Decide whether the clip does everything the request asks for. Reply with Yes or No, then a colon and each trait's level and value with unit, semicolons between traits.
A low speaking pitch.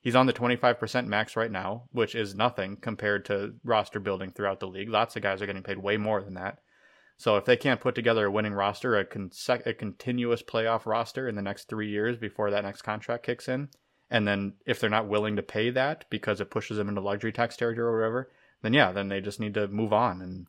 Yes: low, 110 Hz